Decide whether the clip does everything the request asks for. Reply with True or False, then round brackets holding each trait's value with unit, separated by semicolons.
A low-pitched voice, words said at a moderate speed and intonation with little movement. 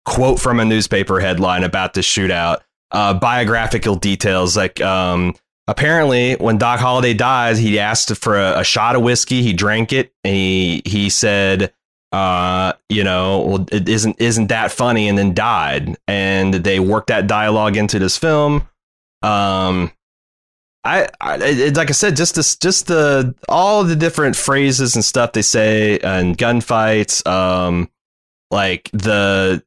False (105 Hz; 160 wpm; 4.3 semitones)